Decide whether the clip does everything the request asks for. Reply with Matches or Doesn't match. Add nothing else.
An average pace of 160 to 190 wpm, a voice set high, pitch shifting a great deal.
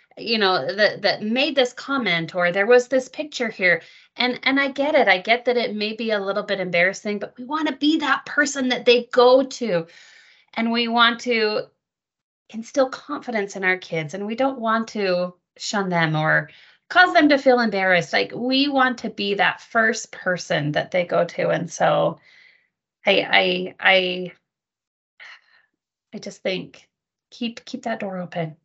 Matches